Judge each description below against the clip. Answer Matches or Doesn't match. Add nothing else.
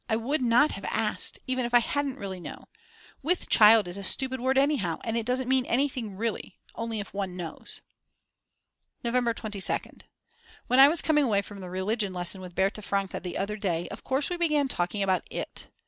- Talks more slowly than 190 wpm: Doesn't match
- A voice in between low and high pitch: Doesn't match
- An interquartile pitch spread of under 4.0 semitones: Doesn't match